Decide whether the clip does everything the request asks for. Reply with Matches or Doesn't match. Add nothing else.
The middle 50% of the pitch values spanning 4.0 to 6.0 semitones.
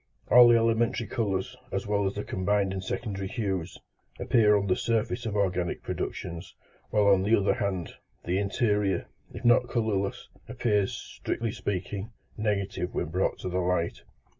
Doesn't match